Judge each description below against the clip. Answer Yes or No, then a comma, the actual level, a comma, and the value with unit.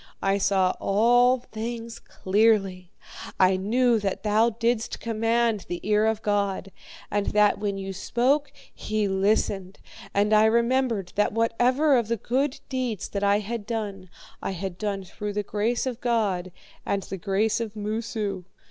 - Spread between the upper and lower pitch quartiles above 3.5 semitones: No, average, 3.0 semitones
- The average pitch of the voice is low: No, high, 215 Hz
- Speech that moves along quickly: No, average, 155 wpm